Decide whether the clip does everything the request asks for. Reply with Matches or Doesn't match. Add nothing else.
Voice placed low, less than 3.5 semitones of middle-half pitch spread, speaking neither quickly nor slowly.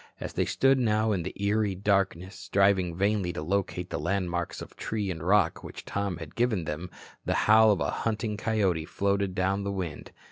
Matches